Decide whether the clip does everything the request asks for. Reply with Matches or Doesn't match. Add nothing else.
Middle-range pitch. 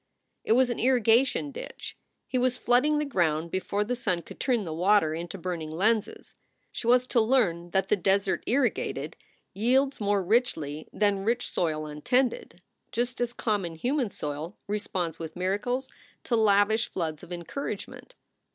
Doesn't match